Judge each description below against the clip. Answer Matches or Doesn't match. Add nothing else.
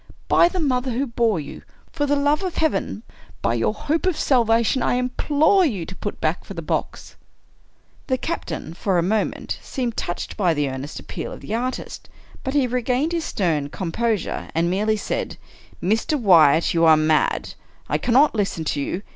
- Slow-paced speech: Doesn't match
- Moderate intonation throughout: Doesn't match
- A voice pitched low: Doesn't match